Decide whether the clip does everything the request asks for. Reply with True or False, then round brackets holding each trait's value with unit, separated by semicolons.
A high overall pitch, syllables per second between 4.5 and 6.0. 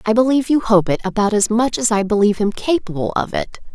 False (220 Hz; 6.3 syllables/s)